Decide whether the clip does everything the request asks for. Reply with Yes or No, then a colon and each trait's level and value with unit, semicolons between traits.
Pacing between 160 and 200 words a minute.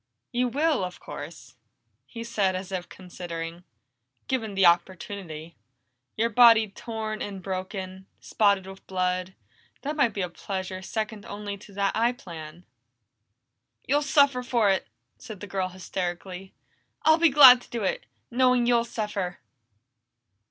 No: average, 140 wpm